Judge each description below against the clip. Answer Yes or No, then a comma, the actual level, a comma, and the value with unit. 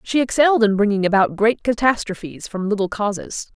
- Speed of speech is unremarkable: Yes, average, 170 wpm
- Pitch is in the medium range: No, high, 210 Hz